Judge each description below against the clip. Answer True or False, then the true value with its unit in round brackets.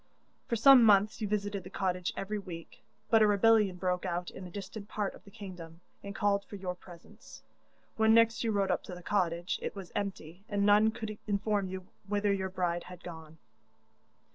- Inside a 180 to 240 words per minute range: True (195 wpm)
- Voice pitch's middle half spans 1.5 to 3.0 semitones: True (2.5 semitones)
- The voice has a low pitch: False (200 Hz)